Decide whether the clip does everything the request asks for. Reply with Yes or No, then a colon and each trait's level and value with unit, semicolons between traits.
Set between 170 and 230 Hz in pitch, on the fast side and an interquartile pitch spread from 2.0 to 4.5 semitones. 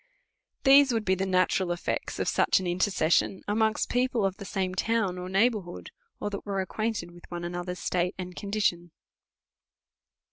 No: high, 190 Hz; average, 165 wpm; average, 3.1 semitones